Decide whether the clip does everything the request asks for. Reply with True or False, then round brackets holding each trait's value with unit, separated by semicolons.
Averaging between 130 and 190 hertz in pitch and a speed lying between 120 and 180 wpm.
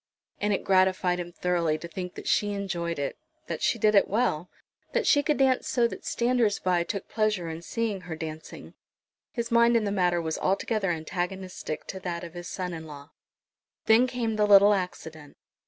False (185 Hz; 190 wpm)